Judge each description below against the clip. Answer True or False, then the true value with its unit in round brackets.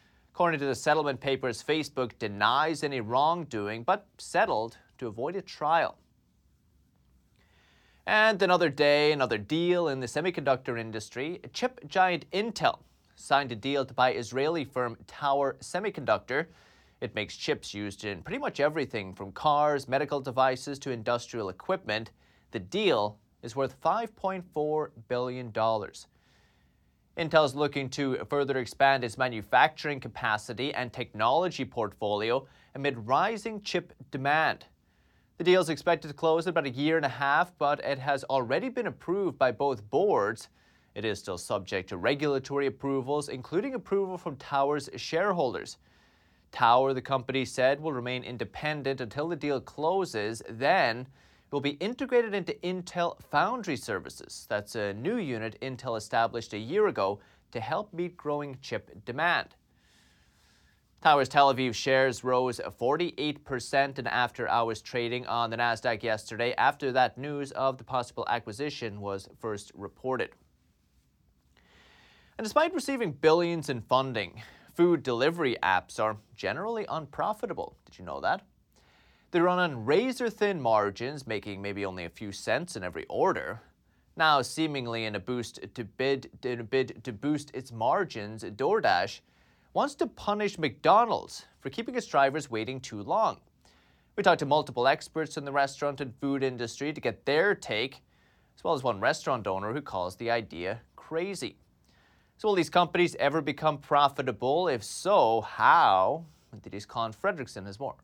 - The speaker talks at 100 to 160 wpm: True (145 wpm)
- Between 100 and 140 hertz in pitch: True (135 Hz)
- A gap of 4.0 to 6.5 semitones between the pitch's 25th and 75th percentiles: True (5.2 semitones)